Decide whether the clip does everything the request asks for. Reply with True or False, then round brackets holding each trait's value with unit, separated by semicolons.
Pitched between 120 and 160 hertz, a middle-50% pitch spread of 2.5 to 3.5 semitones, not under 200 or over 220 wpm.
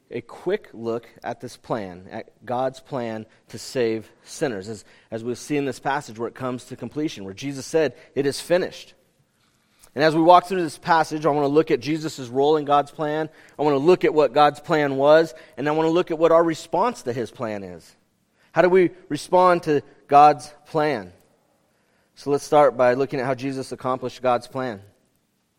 False (140 Hz; 4.6 semitones; 205 wpm)